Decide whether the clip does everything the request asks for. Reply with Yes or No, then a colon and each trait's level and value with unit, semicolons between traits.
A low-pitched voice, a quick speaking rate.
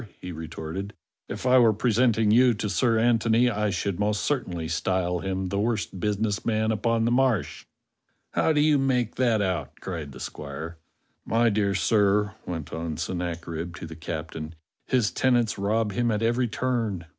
No: low, 105 Hz; average, 170 wpm